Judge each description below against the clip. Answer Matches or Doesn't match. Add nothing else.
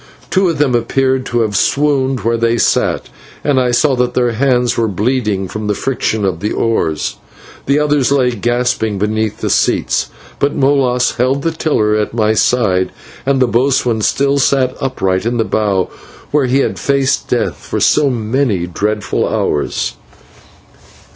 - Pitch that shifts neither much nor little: Matches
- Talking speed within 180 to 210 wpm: Doesn't match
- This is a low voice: Matches